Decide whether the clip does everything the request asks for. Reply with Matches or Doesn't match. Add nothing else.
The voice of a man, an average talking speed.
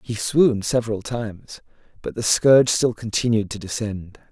Matches